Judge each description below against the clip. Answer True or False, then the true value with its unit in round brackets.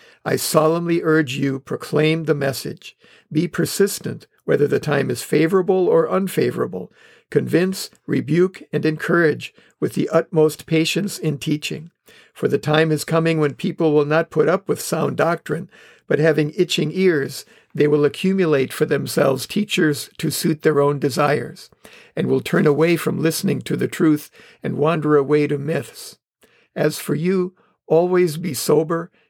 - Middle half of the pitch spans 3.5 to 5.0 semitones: False (2.4 semitones)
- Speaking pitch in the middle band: True (155 Hz)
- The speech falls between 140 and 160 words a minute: True (155 wpm)